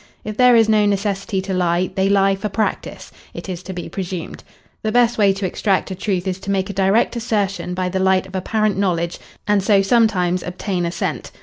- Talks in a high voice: Yes, high, 195 Hz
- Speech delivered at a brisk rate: Yes, fast, 210 wpm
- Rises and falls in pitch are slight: Yes, narrow, 2.1 semitones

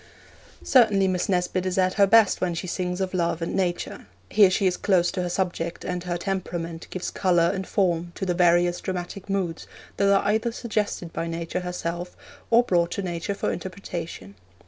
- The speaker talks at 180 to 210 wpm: Yes, average, 190 wpm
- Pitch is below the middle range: No, medium, 180 Hz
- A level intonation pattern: Yes, narrow, 2.1 semitones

